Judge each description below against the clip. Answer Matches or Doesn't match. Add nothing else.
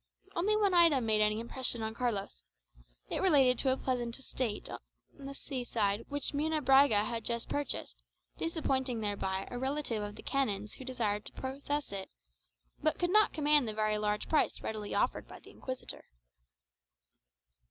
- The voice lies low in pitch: Doesn't match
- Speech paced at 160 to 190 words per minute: Matches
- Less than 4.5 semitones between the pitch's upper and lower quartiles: Doesn't match